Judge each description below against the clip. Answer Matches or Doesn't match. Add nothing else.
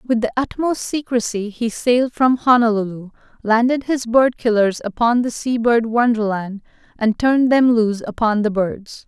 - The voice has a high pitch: Matches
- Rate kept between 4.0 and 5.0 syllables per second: Matches